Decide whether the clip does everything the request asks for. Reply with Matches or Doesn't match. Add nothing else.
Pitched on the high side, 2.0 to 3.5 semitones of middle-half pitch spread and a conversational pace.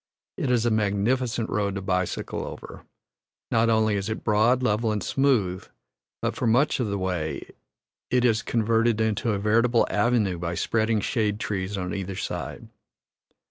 Doesn't match